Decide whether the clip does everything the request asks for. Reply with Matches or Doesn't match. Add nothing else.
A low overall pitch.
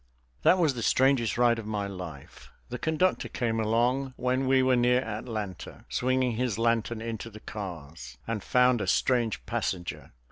Matches